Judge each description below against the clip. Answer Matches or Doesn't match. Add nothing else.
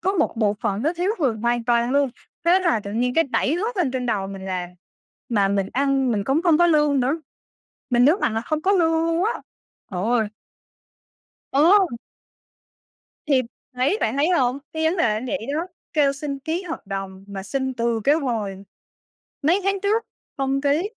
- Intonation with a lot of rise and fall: Matches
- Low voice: Doesn't match